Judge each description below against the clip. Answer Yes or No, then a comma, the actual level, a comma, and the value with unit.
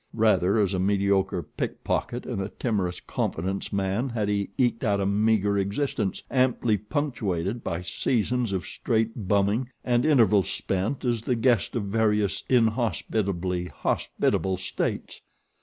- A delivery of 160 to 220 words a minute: No, slow, 135 wpm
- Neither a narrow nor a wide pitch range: Yes, average, 3.4 semitones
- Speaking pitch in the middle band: No, low, 105 Hz